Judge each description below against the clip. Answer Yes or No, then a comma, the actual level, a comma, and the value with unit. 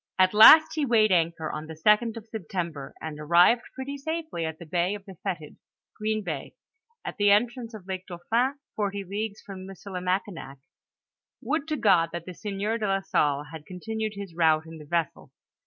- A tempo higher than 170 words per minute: Yes, average, 200 wpm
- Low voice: No, high, 195 Hz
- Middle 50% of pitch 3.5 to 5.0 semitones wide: Yes, average, 4.6 semitones